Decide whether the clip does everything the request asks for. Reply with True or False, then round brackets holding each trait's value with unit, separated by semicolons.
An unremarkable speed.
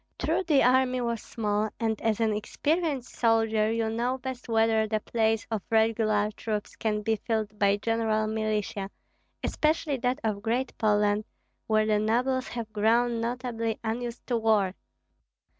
True (150 wpm)